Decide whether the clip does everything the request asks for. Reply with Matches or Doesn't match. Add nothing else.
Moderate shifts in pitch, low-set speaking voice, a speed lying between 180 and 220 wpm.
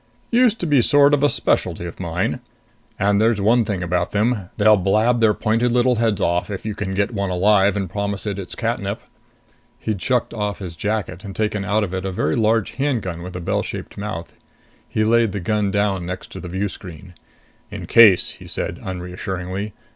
Matches